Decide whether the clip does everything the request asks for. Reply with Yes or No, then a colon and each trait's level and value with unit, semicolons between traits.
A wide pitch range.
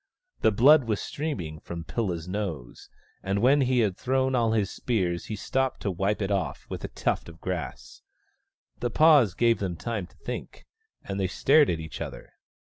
Yes: wide, 5.9 semitones